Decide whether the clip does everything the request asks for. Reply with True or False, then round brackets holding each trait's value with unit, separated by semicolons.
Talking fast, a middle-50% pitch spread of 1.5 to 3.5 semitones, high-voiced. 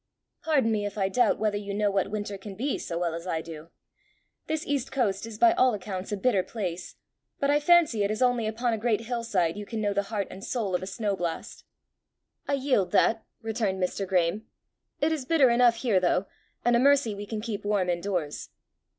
False (225 wpm; 4.0 semitones; 210 Hz)